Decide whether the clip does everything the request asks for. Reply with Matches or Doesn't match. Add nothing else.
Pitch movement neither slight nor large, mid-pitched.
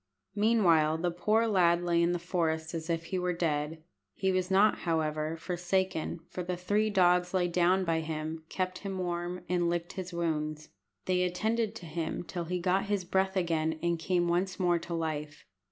Doesn't match